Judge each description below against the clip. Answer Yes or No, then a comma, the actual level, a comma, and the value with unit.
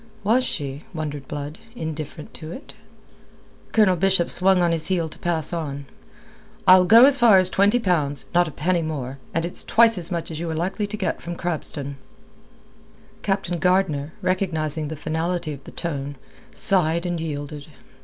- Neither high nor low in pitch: Yes, medium, 170 Hz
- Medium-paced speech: Yes, average, 170 wpm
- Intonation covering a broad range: No, average, 3.4 semitones